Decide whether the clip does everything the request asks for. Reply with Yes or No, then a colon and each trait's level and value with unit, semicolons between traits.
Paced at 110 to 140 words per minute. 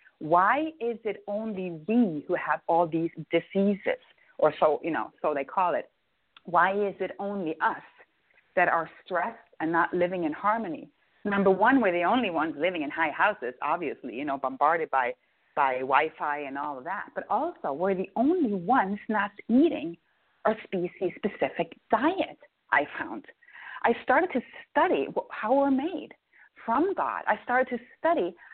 No: average, 165 wpm